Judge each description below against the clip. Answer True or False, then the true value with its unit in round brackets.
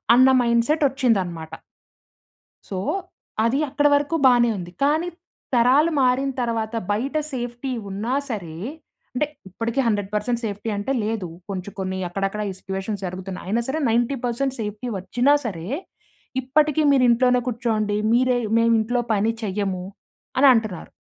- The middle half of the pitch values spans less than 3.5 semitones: False (4.1 semitones)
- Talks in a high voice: True (230 Hz)